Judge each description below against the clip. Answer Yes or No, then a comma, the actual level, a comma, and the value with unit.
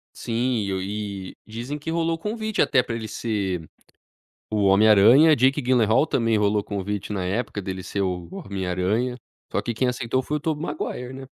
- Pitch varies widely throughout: No, average, 4.7 semitones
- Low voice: Yes, low, 110 Hz